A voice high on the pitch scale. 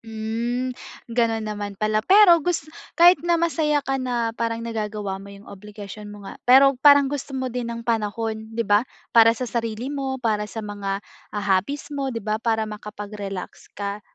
Yes: high, 225 Hz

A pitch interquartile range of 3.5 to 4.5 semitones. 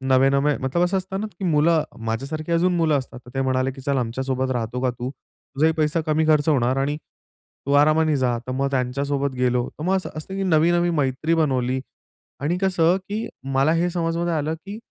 Yes: average, 4.0 semitones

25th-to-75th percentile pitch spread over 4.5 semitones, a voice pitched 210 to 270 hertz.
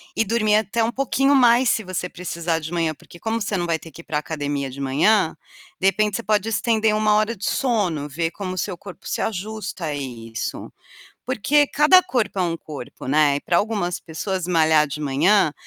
No: wide, 5.6 semitones; medium, 185 Hz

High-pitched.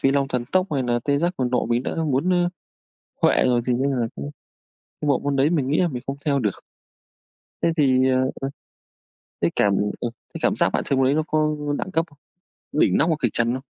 No: low, 135 Hz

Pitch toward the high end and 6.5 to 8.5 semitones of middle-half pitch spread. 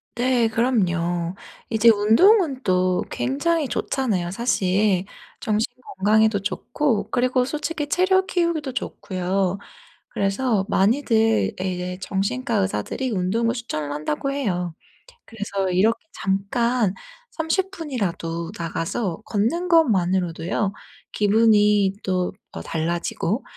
No: high, 210 Hz; wide, 5.5 semitones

